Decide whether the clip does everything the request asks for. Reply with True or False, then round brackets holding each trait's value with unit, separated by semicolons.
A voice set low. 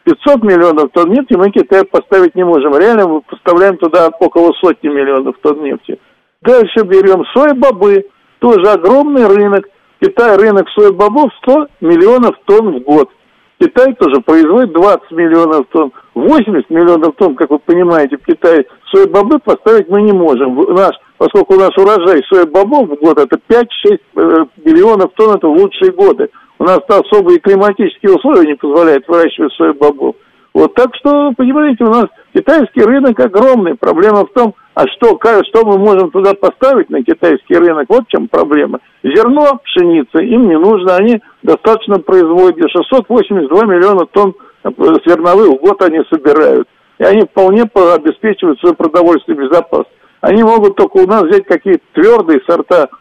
False (225 Hz)